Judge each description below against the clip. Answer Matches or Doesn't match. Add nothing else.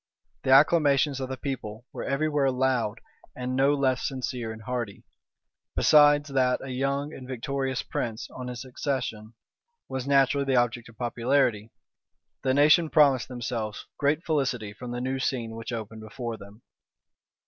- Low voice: Matches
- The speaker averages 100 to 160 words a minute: Matches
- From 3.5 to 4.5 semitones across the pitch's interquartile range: Doesn't match